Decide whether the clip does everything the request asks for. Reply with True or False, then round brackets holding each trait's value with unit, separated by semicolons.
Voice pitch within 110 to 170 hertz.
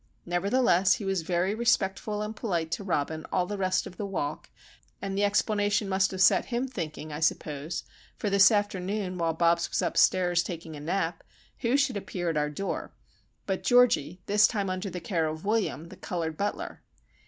False (185 Hz)